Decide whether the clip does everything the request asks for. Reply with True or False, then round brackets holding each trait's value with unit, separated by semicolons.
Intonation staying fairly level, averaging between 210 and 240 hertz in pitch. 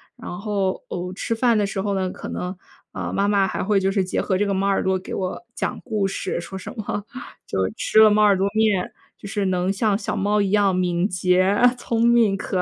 False (2.0 semitones; 195 Hz)